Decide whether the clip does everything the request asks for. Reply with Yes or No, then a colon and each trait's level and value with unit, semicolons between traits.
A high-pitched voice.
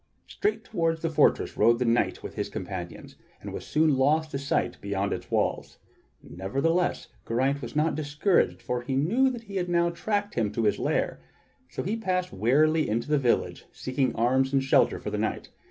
No: medium, 145 Hz